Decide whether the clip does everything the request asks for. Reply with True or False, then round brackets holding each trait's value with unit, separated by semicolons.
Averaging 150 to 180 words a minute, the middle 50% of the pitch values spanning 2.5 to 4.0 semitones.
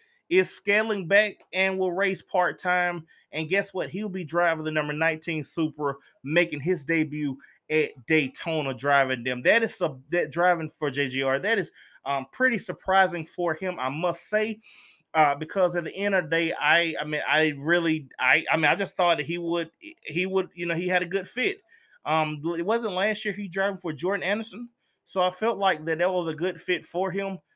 False (205 wpm; 3.7 semitones)